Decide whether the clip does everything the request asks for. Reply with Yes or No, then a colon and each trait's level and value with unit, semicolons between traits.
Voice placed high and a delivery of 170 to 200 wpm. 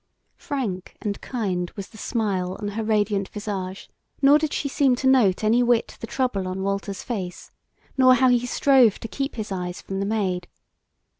Yes: high, 215 Hz; average, 180 wpm